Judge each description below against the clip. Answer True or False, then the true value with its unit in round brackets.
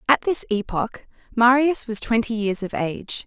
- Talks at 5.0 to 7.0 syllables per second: False (4.6 syllables/s)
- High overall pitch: True (225 Hz)